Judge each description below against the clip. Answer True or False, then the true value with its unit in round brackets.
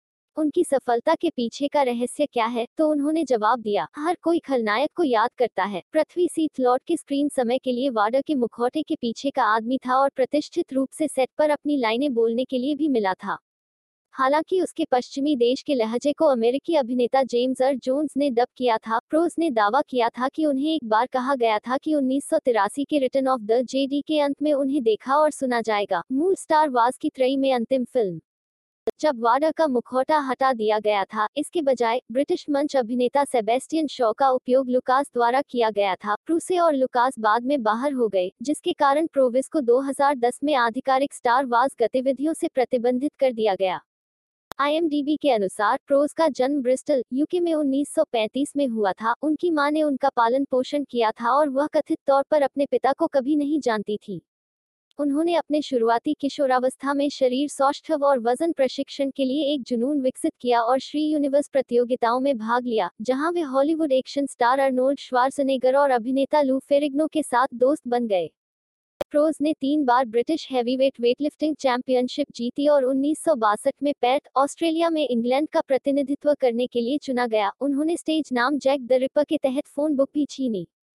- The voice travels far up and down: False (3.2 semitones)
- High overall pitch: True (270 Hz)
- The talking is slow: False (185 wpm)